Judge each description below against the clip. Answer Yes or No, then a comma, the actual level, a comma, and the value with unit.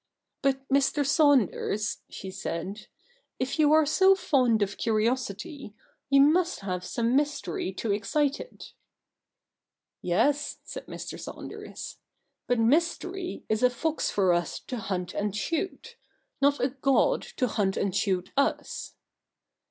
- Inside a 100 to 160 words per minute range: Yes, slow, 135 wpm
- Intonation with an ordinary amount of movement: No, wide, 6.5 semitones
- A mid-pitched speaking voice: No, very high, 255 Hz